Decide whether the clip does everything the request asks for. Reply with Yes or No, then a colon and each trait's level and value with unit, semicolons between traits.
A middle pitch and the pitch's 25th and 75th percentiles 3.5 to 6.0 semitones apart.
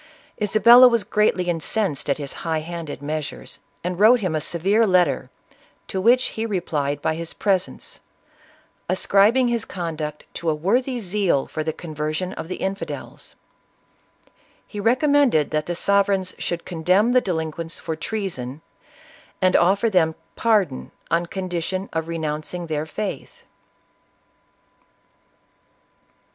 Yes: medium, 180 Hz; average, 4.7 semitones